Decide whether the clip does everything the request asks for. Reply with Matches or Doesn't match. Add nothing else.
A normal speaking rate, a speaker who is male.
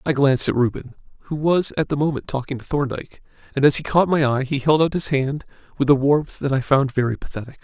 Doesn't match